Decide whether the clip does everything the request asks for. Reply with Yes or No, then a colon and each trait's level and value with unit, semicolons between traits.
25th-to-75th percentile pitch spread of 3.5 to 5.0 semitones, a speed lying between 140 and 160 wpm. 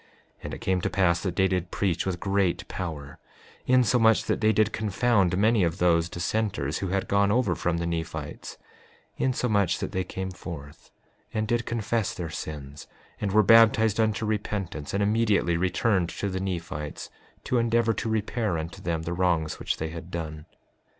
No: average, 4.3 semitones; average, 175 wpm